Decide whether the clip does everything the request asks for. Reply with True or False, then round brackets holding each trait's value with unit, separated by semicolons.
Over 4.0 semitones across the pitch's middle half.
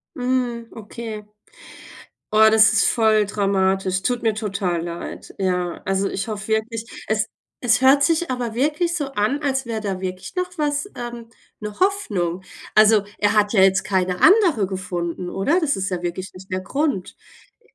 True (4.8 semitones)